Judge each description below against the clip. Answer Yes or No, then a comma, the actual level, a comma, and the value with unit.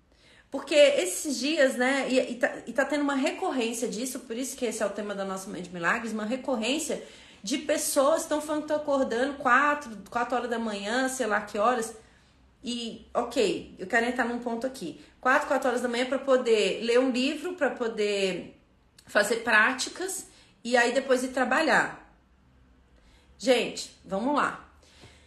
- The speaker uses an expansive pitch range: No, average, 3.8 semitones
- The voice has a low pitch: No, very high, 250 Hz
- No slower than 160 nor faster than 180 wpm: Yes, average, 175 wpm